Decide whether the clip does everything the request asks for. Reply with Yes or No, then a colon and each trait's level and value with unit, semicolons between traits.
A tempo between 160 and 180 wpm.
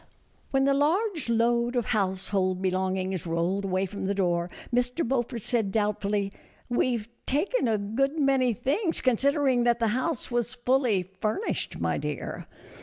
Yes: average, 165 wpm